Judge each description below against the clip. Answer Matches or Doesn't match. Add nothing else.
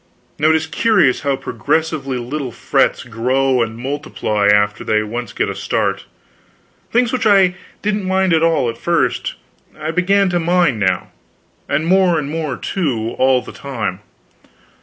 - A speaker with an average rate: Matches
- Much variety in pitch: Matches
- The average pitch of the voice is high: Doesn't match